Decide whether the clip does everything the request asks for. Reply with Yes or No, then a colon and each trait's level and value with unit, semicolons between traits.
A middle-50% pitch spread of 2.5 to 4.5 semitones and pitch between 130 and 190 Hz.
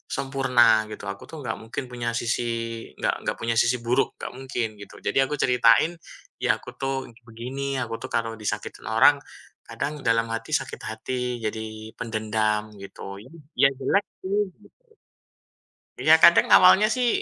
No: average, 3.3 semitones; low, 120 Hz